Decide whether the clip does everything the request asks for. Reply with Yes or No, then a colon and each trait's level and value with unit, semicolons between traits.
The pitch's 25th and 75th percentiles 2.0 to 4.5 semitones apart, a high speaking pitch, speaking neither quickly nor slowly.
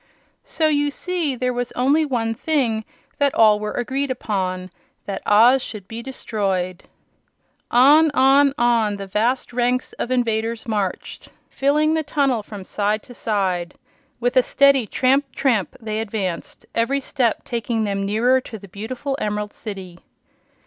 Yes: average, 4.2 semitones; high, 235 Hz; average, 150 wpm